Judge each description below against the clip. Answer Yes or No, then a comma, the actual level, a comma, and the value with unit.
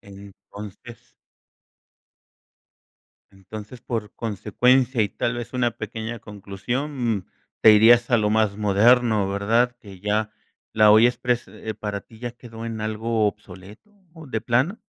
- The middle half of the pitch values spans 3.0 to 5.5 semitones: No, narrow, 2.5 semitones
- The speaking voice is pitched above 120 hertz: No, low, 110 Hz